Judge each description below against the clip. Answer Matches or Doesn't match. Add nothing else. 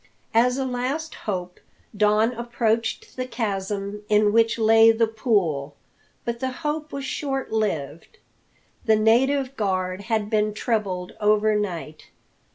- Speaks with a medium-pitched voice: Doesn't match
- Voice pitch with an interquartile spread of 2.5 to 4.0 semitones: Matches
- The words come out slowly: Matches